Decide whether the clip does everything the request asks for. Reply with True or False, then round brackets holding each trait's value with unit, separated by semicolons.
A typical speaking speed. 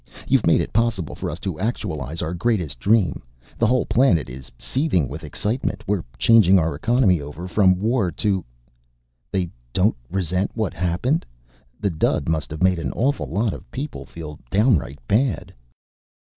True (165 wpm)